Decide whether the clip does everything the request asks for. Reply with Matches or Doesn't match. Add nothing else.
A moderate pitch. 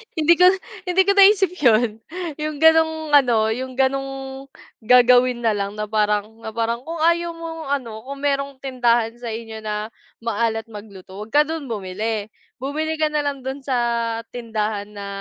Doesn't match